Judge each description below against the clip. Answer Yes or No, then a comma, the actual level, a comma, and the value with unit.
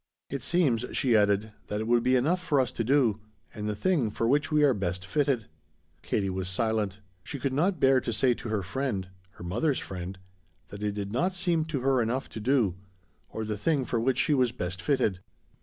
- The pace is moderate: No, fast, 215 wpm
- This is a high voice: No, low, 120 Hz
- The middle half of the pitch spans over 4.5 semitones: Yes, average, 5.1 semitones